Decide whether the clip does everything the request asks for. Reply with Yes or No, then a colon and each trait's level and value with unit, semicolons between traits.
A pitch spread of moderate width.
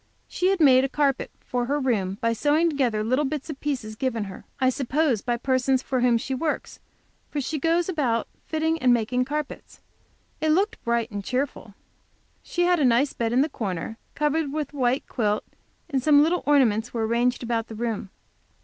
Yes: average, 4.2 semitones